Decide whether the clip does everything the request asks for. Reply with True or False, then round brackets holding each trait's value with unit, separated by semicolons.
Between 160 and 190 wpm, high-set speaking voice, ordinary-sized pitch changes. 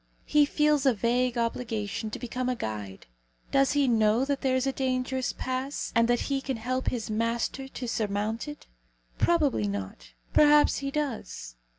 True (170 wpm; 250 Hz; 3.7 semitones)